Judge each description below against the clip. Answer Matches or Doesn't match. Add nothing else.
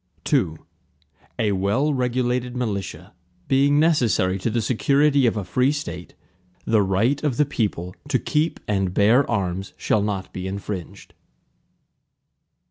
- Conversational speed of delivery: Doesn't match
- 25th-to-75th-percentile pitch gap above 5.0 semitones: Matches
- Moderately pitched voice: Doesn't match